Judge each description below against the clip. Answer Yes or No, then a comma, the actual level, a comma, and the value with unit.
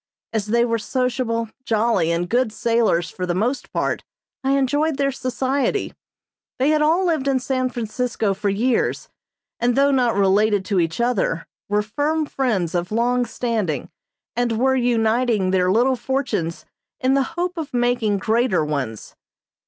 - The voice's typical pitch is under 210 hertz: No, high, 235 Hz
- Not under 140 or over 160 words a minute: Yes, average, 155 wpm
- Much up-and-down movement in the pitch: No, average, 4.3 semitones